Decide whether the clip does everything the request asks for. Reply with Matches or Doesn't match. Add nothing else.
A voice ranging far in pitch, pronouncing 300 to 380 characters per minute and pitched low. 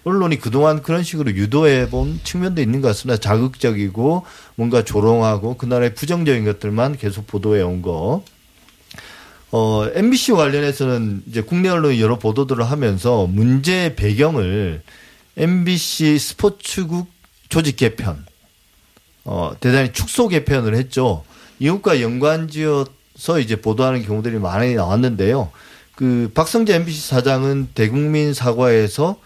Matches